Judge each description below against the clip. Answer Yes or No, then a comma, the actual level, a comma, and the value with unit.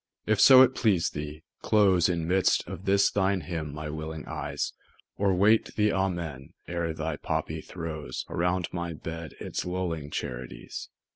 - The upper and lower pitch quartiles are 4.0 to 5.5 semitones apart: No, average, 3.6 semitones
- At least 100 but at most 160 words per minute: Yes, average, 155 wpm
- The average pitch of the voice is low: Yes, very low, 85 Hz